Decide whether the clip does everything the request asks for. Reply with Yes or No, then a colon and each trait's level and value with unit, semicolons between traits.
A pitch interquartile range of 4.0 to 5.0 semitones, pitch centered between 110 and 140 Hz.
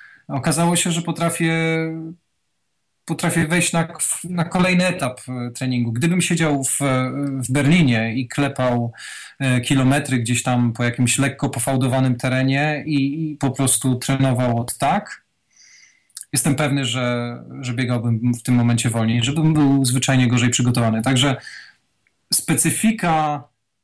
Yes: average, 4.3 semitones; low, 135 Hz